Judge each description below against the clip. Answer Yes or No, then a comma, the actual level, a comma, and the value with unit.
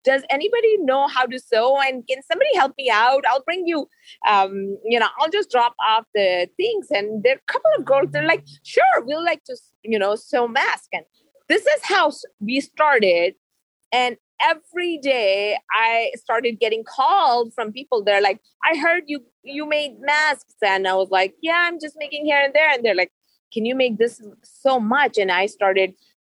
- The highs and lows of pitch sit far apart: Yes, wide, 5.9 semitones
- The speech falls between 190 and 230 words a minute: Yes, average, 200 wpm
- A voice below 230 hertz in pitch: No, very high, 260 Hz